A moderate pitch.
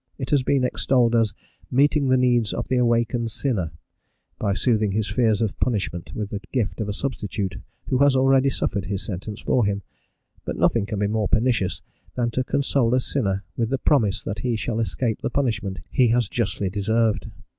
No: low, 115 Hz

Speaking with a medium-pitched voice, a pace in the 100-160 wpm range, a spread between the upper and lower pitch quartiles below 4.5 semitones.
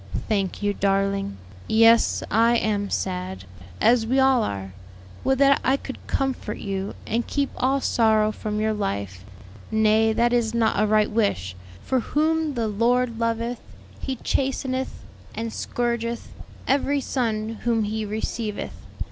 No: high, 225 Hz; average, 140 wpm; average, 2.9 semitones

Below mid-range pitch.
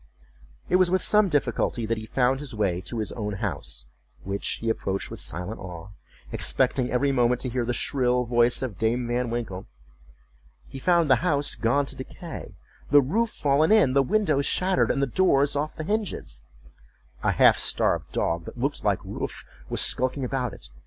Yes: low, 125 Hz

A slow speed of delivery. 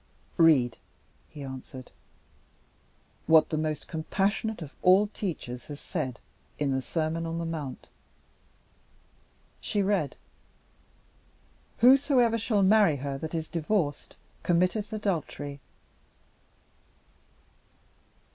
Yes: slow, 95 wpm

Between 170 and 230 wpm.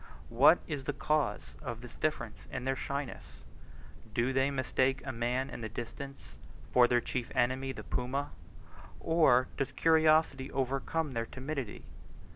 No: average, 145 wpm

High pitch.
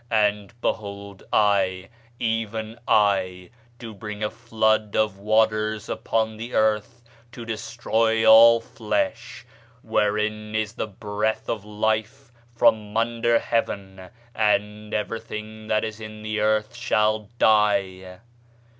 No: low, 110 Hz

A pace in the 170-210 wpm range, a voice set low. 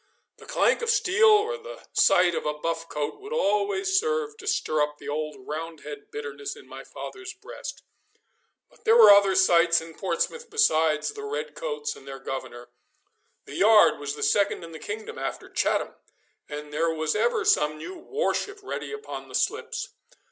No: average, 180 wpm; high, 190 Hz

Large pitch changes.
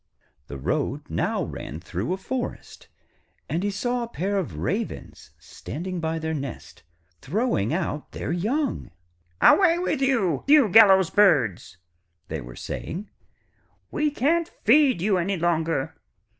Yes: wide, 7.4 semitones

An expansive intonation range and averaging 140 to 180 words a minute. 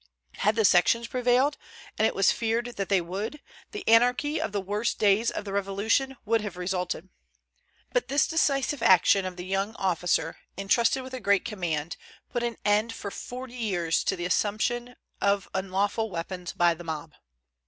No: average, 4.3 semitones; average, 175 wpm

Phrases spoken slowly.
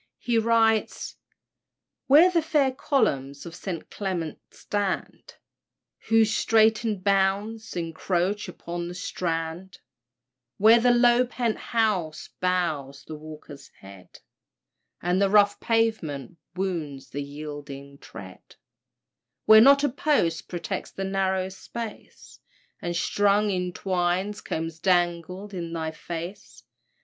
Yes: slow, 115 wpm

